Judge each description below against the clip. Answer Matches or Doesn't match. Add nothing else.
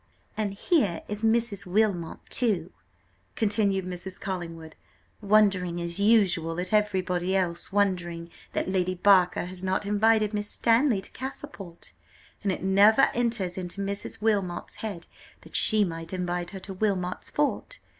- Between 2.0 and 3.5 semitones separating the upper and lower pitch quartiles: Matches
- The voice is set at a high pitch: Matches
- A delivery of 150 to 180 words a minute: Doesn't match